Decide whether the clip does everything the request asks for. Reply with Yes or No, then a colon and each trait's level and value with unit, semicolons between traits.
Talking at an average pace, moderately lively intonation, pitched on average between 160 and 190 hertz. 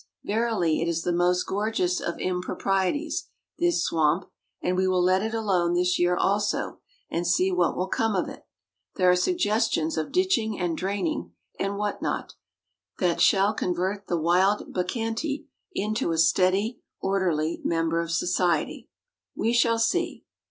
Yes: average, 150 wpm; average, 3.5 semitones; medium, 185 Hz